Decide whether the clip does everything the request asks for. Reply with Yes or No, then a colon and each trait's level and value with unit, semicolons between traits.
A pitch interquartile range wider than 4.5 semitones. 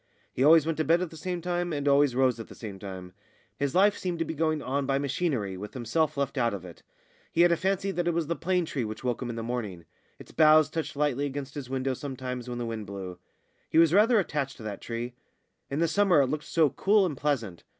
Yes: wide, 5.4 semitones